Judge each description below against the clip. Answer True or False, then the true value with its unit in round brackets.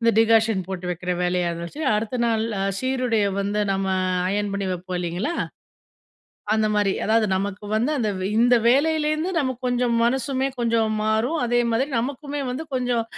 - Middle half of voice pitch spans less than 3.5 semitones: False (4.0 semitones)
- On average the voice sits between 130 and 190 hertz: False (230 Hz)